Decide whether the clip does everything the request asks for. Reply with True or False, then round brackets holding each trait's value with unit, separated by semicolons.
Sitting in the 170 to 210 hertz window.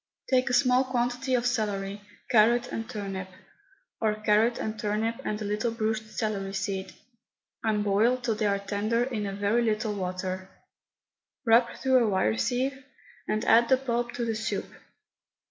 False (220 Hz)